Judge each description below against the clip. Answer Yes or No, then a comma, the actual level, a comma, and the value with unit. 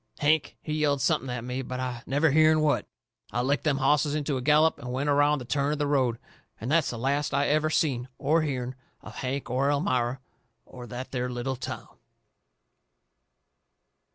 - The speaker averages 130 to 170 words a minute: No, average, 185 wpm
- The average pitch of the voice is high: No, medium, 140 Hz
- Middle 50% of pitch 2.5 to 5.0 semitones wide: Yes, average, 2.9 semitones